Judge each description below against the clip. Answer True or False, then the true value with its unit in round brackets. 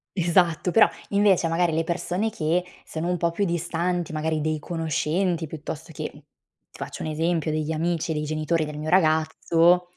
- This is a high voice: False (165 Hz)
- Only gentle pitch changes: True (2.0 semitones)